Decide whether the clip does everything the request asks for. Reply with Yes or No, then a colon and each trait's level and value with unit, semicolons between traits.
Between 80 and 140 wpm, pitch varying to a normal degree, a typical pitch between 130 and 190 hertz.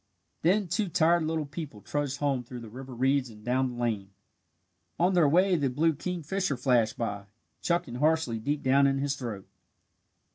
No: average, 175 wpm; average, 4.9 semitones; medium, 140 Hz